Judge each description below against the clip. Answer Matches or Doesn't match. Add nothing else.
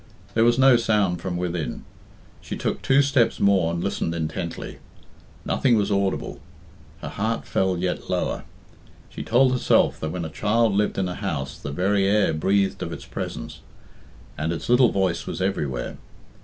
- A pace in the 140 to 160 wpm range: Doesn't match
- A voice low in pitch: Matches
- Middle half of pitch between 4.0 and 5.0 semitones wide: Matches